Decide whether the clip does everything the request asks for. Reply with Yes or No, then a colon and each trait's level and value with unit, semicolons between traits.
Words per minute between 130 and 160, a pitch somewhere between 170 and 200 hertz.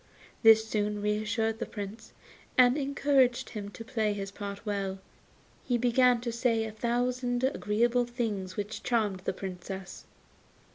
No: average, 145 wpm; high, 225 Hz